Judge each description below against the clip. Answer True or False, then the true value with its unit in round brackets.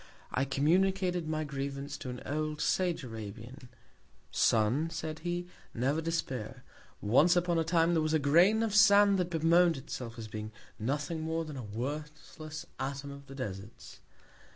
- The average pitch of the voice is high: False (150 Hz)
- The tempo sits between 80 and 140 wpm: False (155 wpm)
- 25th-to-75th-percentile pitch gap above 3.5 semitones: True (4.5 semitones)